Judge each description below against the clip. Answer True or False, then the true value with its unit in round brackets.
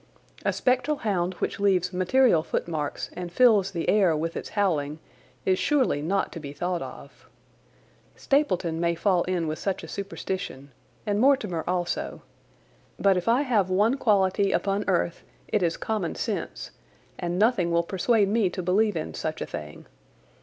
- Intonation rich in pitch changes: False (3.7 semitones)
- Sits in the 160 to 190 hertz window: True (185 Hz)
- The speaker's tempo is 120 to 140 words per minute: False (160 wpm)